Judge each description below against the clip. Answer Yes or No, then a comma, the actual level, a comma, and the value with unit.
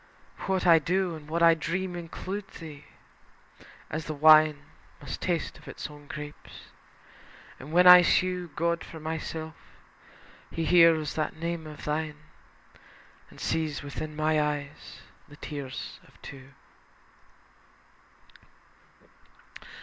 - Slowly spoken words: Yes, slow, 120 wpm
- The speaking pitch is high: No, medium, 160 Hz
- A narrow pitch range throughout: Yes, narrow, 2.1 semitones